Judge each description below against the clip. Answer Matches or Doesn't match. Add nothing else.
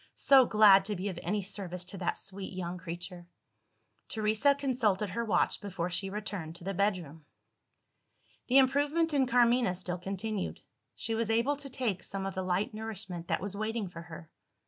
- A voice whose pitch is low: Doesn't match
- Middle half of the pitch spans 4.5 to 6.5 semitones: Doesn't match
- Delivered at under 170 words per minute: Doesn't match